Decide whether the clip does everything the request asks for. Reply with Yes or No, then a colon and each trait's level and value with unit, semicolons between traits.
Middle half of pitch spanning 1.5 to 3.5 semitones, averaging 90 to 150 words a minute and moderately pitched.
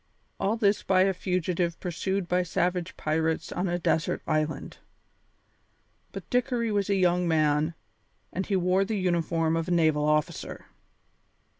Yes: average, 2.8 semitones; average, 145 wpm; medium, 180 Hz